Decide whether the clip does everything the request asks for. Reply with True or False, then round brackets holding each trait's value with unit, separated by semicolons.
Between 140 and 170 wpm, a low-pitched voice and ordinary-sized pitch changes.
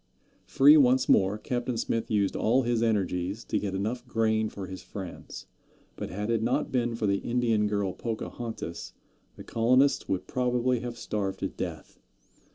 True (165 wpm; 115 Hz; 3.3 semitones)